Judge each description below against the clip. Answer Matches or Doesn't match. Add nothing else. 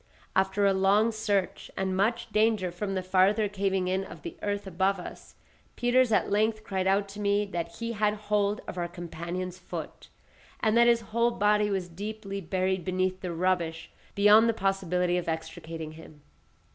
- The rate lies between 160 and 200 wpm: Matches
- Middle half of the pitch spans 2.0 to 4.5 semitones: Matches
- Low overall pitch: Doesn't match